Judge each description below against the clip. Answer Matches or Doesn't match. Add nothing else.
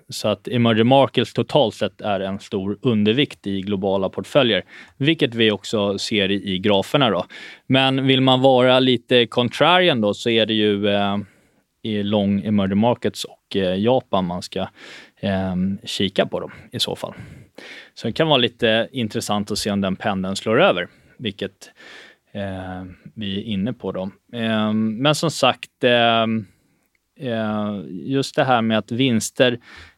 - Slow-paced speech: Doesn't match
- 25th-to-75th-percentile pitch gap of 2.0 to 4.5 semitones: Matches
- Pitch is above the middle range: Doesn't match